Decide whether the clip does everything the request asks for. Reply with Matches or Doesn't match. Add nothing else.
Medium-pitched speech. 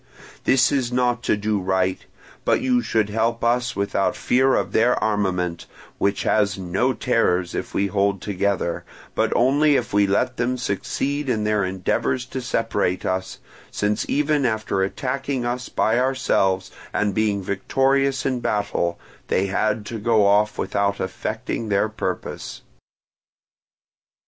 Doesn't match